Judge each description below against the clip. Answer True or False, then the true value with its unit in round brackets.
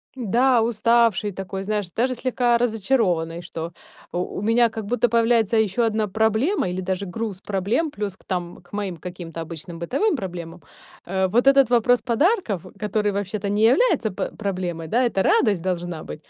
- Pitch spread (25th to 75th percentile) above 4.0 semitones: True (4.5 semitones)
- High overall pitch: True (210 Hz)